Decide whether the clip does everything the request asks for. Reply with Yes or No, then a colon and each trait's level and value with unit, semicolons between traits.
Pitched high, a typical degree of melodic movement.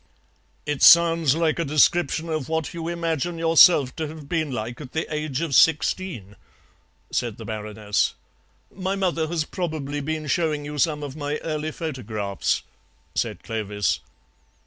No: medium, 155 Hz; average, 3.6 semitones